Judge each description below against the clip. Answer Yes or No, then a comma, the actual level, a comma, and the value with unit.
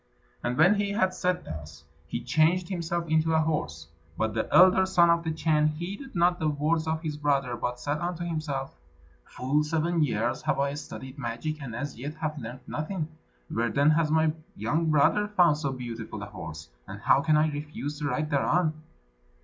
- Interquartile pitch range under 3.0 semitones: No, average, 4.0 semitones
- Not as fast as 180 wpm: No, average, 190 wpm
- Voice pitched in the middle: Yes, medium, 150 Hz